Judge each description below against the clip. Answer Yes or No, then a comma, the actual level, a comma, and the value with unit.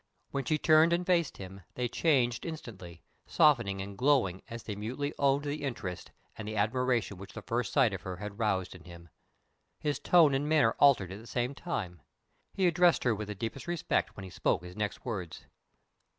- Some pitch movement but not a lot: No, wide, 6.7 semitones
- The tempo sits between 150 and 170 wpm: No, average, 195 wpm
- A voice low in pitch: Yes, low, 115 Hz